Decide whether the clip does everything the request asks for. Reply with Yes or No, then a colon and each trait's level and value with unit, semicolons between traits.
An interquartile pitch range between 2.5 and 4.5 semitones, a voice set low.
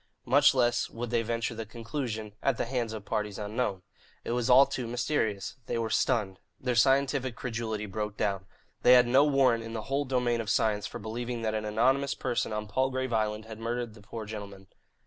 Yes: average, 2.8 semitones; low, 115 Hz